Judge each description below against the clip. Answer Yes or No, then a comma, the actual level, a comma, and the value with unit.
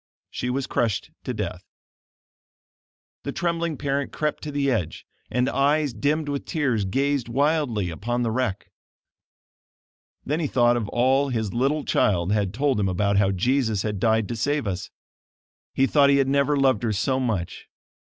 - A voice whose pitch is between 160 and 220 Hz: No, low, 125 Hz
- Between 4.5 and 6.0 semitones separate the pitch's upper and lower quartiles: Yes, average, 4.9 semitones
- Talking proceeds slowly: No, average, 165 wpm